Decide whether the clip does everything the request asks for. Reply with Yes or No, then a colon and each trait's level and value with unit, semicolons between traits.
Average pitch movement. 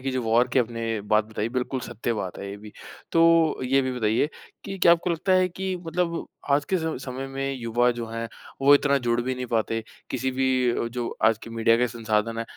Yes: average, 3.5 semitones